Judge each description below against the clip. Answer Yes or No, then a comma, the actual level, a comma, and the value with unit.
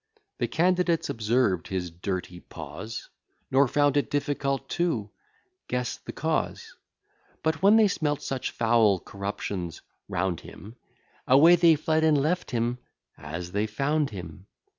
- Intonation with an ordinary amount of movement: No, wide, 7.6 semitones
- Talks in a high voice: No, low, 125 Hz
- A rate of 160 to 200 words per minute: No, slow, 135 wpm